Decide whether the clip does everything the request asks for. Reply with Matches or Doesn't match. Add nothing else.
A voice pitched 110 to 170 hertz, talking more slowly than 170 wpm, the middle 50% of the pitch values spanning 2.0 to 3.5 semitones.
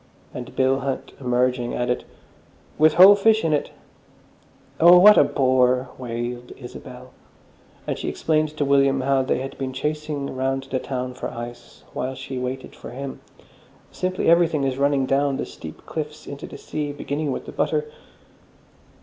Matches